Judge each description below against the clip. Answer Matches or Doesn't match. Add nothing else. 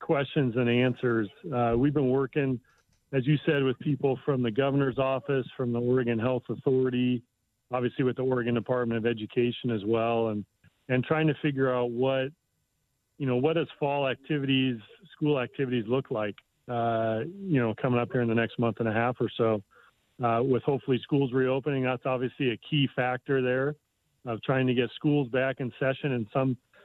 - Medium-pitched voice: Doesn't match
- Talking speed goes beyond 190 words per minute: Doesn't match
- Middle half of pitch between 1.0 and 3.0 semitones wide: Matches